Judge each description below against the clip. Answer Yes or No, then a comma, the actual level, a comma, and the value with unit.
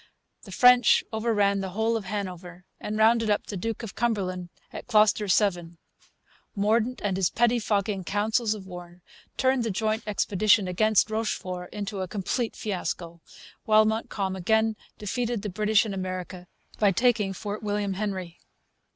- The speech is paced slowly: No, average, 150 wpm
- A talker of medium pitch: No, high, 205 Hz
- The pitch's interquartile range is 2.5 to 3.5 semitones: Yes, average, 2.8 semitones